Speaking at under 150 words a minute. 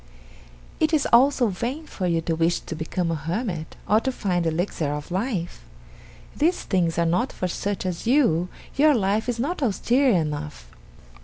No: average, 175 wpm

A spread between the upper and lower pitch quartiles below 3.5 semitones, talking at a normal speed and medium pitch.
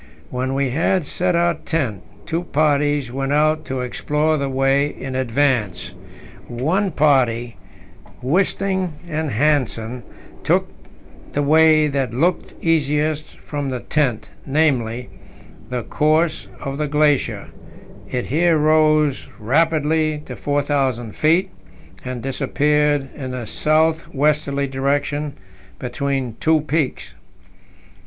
No: average, 3.0 semitones; slow, 115 wpm; medium, 145 Hz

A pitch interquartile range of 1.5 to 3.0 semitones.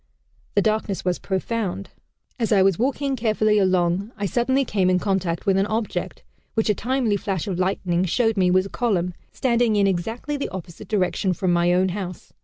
No: average, 3.4 semitones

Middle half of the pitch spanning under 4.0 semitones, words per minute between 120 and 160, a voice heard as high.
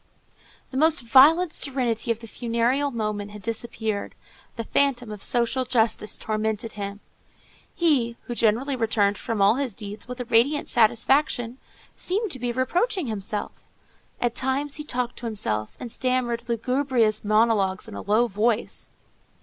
Yes: average, 3.2 semitones; average, 150 wpm; high, 235 Hz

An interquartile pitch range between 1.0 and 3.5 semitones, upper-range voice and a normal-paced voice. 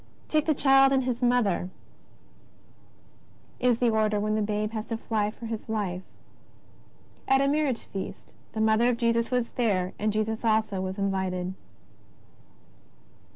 Yes: average, 3.0 semitones; high, 220 Hz; average, 155 wpm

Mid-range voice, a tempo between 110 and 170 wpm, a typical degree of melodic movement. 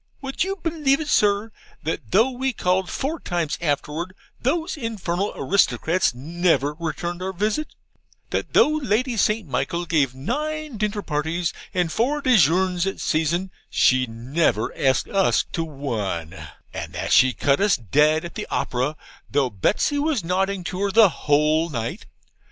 No: medium, 175 Hz; average, 150 wpm; wide, 6.9 semitones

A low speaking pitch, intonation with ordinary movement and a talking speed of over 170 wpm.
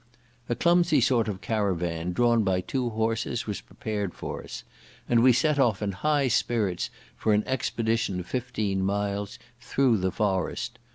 No: low, 110 Hz; average, 3.8 semitones; average, 160 wpm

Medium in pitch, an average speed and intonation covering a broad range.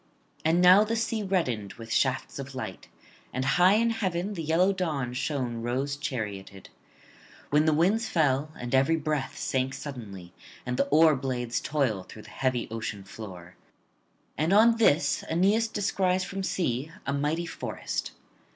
Yes: medium, 145 Hz; average, 155 wpm; wide, 6.7 semitones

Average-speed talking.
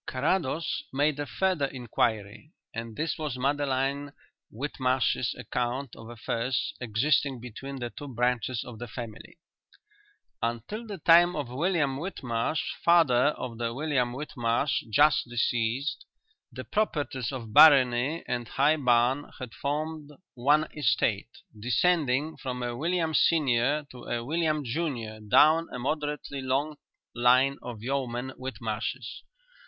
No: slow, 125 wpm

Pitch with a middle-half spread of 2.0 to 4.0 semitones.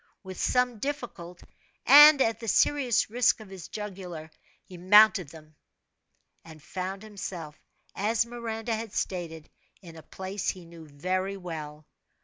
No: average, 4.9 semitones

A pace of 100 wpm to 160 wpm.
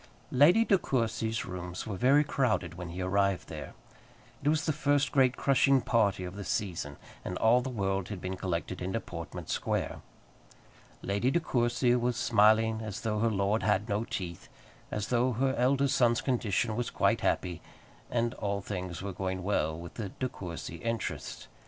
No: average, 175 wpm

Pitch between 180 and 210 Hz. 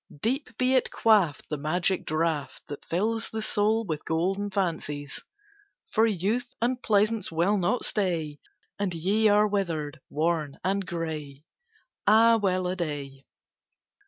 Yes: medium, 185 Hz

